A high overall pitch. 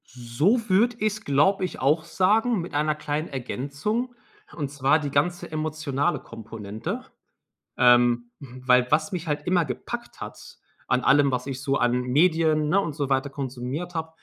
No: medium, 145 Hz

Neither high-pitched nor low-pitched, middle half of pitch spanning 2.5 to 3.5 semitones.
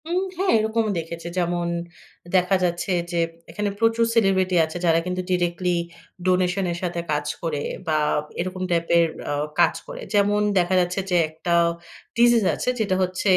Yes: medium, 180 Hz; average, 3.1 semitones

